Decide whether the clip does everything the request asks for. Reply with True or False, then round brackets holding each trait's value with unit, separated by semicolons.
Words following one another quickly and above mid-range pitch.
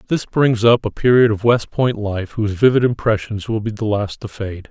False (230 wpm; 110 Hz)